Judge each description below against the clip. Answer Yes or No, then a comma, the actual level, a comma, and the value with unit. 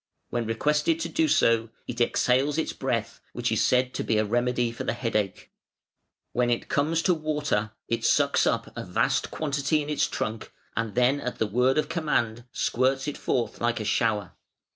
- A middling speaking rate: Yes, average, 185 wpm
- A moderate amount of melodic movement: Yes, average, 4.4 semitones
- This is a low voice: Yes, low, 125 Hz